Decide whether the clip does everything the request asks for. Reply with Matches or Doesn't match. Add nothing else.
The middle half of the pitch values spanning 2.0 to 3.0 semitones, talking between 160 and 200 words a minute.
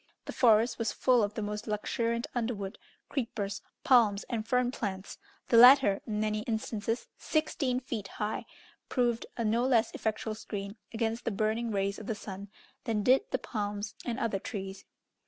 Matches